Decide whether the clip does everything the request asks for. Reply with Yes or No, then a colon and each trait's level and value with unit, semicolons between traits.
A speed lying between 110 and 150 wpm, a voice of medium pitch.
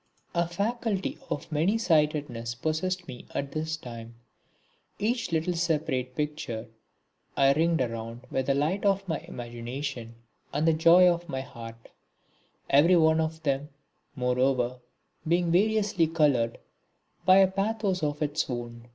Yes: slow, 135 wpm; medium, 155 Hz